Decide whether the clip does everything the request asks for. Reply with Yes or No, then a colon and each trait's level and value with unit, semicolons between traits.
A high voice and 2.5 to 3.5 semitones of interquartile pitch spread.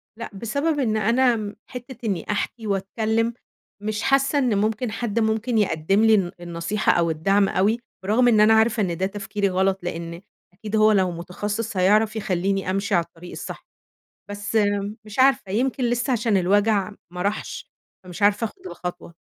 Yes: high, 210 Hz; average, 3.0 semitones